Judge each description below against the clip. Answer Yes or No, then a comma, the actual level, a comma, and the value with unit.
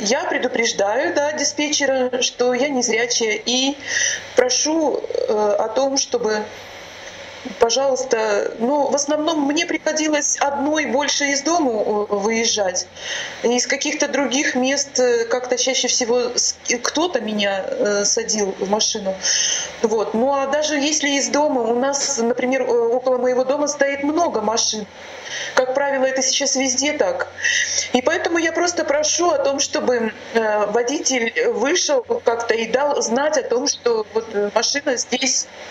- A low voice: No, very high, 265 Hz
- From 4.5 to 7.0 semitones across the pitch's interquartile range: No, average, 3.6 semitones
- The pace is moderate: Yes, average, 135 wpm